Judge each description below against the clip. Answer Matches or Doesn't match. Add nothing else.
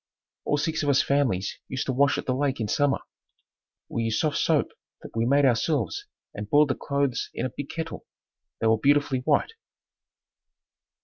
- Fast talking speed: Doesn't match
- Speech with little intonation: Doesn't match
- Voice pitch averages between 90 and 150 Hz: Matches